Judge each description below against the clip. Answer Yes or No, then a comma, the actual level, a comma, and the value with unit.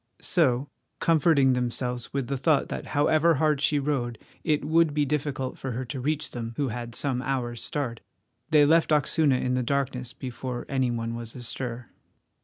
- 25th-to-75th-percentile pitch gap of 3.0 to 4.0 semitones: Yes, average, 3.3 semitones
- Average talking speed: Yes, average, 175 wpm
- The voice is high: No, low, 135 Hz